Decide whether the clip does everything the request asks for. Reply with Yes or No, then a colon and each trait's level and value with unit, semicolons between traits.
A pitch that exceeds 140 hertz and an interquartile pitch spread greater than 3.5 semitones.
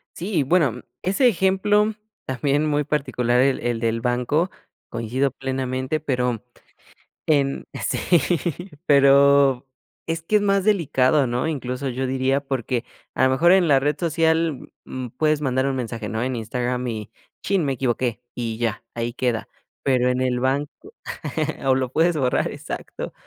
No: low, 135 Hz; average, 3.9 semitones